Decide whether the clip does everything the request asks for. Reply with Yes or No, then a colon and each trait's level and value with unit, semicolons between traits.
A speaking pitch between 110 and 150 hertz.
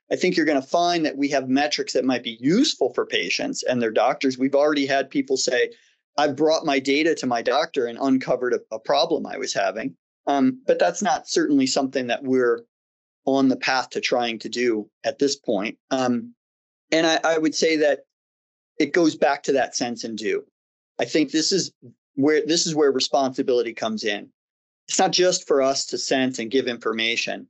Yes: medium, 140 Hz